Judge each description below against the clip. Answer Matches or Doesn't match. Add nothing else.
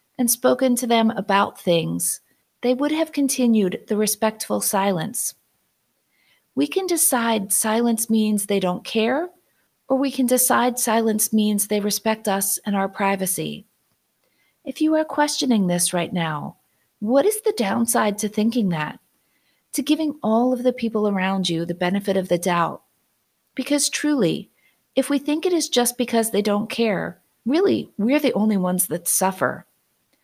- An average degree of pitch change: Matches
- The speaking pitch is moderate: Doesn't match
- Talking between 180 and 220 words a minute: Doesn't match